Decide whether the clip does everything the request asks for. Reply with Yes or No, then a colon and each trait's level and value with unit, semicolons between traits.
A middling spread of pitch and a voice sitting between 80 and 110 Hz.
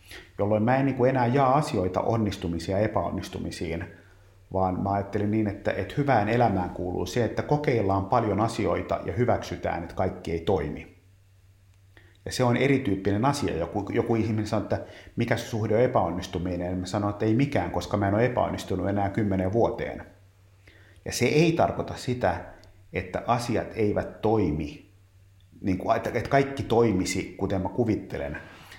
Yes: average, 3.5 semitones; low, 100 Hz